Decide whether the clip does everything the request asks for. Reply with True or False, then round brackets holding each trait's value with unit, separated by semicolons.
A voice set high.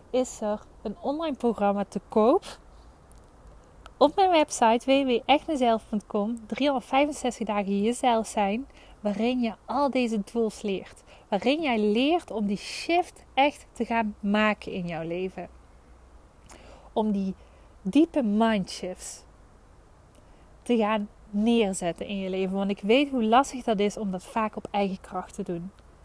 True (215 Hz)